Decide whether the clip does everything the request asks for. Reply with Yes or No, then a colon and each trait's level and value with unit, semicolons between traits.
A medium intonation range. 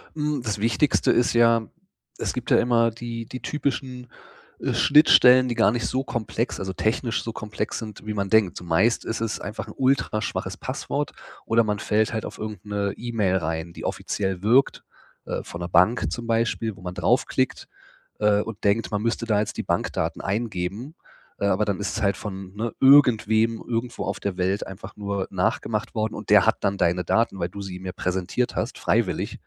Yes: average, 3.1 semitones